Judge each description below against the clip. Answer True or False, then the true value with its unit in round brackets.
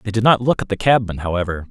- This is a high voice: False (105 Hz)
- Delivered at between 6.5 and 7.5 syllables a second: True (7.0 syllables/s)